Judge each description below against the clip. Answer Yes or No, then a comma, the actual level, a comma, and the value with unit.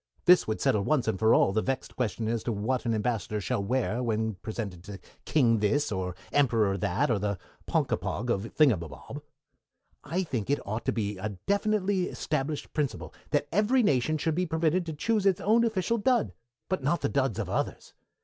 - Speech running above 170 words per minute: Yes, average, 190 wpm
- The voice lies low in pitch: Yes, low, 125 Hz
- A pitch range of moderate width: No, wide, 7.5 semitones